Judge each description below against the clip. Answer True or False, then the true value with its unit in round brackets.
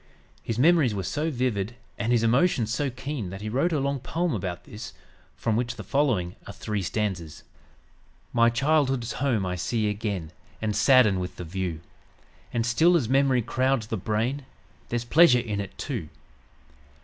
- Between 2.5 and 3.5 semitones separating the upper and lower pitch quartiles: False (4.5 semitones)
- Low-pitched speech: True (115 Hz)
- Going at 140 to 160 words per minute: False (170 wpm)